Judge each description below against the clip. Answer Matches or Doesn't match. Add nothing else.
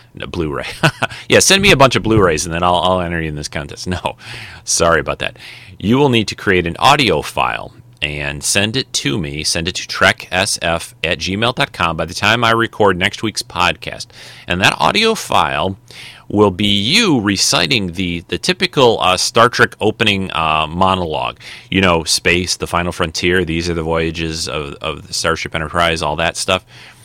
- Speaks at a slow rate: Doesn't match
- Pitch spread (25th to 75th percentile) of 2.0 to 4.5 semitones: Doesn't match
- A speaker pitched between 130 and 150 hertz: Doesn't match